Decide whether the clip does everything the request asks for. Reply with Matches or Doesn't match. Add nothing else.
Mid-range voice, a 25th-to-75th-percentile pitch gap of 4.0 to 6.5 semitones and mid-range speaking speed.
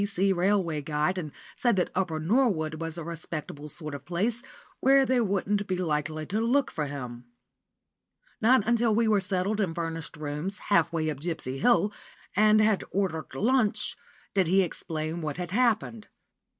Matches